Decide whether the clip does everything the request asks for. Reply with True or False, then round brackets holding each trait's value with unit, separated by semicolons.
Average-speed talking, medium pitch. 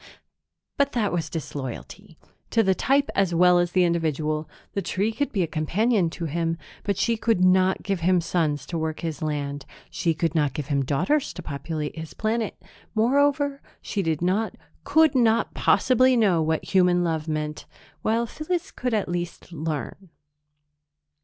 True (165 wpm; 175 Hz)